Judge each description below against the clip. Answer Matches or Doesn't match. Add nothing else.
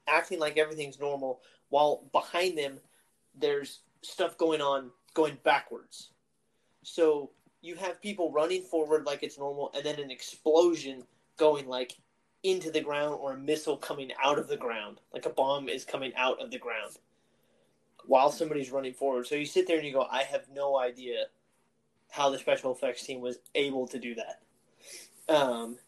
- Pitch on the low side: Doesn't match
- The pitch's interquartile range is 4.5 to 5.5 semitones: Doesn't match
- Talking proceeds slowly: Doesn't match